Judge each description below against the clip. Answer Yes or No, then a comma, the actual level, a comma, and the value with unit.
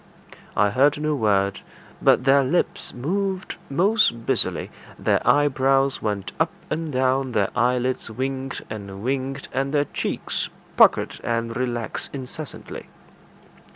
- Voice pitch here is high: No, low, 130 Hz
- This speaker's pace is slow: Yes, slow, 120 wpm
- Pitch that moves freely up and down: No, average, 3.2 semitones